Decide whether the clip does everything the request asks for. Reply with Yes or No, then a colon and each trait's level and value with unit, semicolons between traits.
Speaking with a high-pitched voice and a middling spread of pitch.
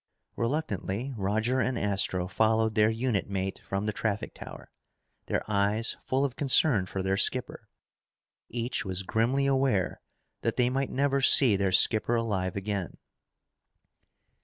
No: low, 110 Hz; average, 4.5 semitones